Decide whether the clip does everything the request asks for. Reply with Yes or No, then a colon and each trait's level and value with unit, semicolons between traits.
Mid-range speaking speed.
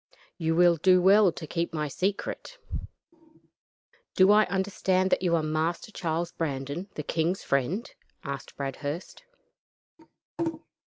No: slow, 120 wpm